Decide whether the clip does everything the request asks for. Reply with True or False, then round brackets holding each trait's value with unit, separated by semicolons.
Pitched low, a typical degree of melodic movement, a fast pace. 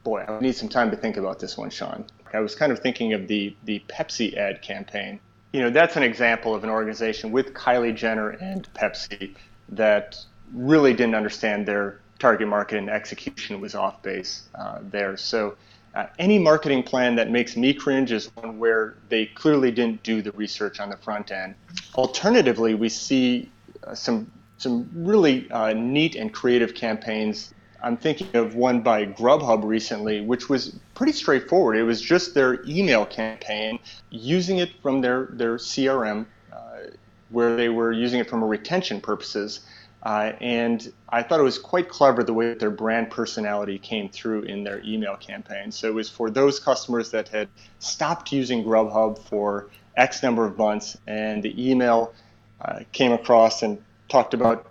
False (115 Hz; 3.2 semitones; 175 wpm)